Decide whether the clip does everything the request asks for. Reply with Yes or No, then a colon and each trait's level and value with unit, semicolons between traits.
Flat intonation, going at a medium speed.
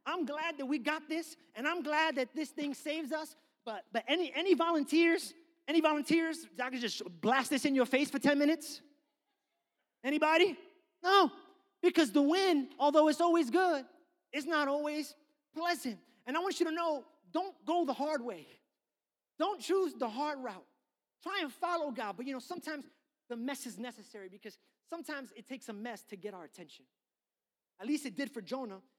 No: average, 4.2 semitones; average, 185 wpm